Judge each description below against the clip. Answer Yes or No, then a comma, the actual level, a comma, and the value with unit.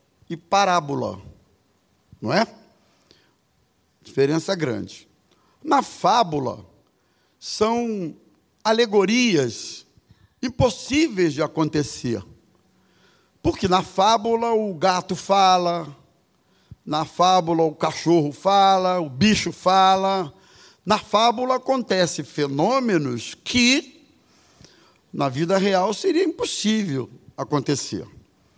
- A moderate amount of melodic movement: No, wide, 6.2 semitones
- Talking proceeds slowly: Yes, slow, 85 wpm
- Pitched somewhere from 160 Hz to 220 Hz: Yes, medium, 185 Hz